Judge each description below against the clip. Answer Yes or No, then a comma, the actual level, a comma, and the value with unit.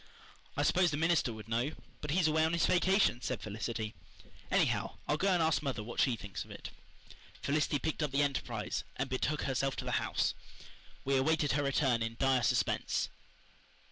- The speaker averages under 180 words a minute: No, average, 185 wpm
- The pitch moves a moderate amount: Yes, average, 4.7 semitones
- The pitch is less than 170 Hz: Yes, medium, 140 Hz